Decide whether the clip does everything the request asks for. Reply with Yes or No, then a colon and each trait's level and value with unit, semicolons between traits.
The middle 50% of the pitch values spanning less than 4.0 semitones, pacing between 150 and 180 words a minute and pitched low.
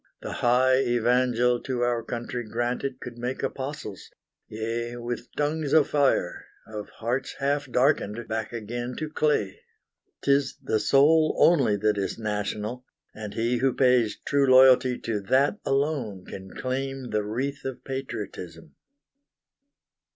No: average, 3.5 semitones; slow, 135 wpm; low, 125 Hz